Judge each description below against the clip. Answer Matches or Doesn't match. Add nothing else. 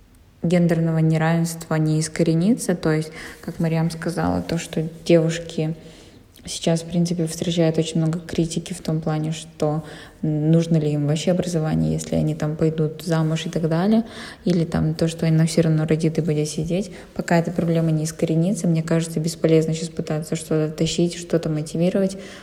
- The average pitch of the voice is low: Doesn't match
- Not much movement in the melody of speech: Matches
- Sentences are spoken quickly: Matches